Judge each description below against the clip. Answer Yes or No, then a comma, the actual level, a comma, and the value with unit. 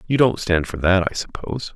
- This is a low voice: Yes, low, 100 Hz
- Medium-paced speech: No, fast, 240 wpm